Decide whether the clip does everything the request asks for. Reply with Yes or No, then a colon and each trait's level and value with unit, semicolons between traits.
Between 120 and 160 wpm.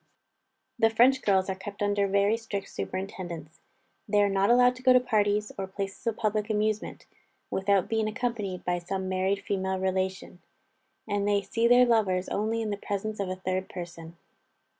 No: average, 175 wpm